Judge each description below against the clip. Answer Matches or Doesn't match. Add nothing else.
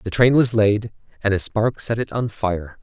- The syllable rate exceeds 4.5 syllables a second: Doesn't match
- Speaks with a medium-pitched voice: Doesn't match